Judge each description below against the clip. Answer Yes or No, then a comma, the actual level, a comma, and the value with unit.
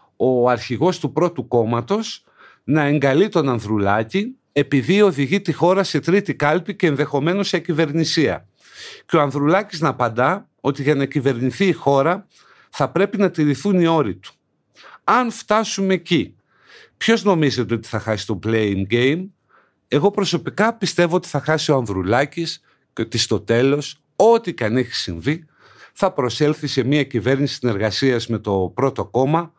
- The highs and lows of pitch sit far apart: Yes, wide, 6.0 semitones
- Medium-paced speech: Yes, average, 155 wpm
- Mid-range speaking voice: Yes, medium, 145 Hz